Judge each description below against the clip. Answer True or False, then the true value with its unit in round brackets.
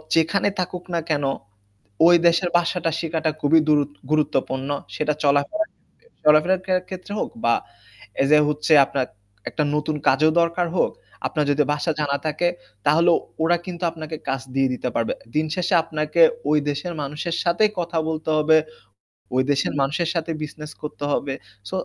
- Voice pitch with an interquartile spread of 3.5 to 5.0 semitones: False (2.6 semitones)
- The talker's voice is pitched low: False (155 Hz)